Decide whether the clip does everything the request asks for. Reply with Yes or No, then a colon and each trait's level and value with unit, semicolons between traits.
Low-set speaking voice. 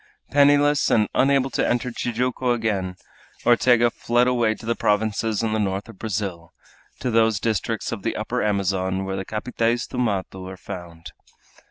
Yes: low, 110 Hz